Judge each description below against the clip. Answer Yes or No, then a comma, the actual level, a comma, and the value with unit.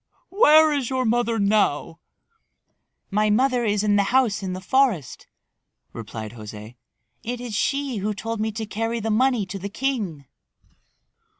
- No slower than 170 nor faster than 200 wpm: No, average, 155 wpm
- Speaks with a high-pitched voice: Yes, high, 215 Hz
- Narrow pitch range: No, average, 4.0 semitones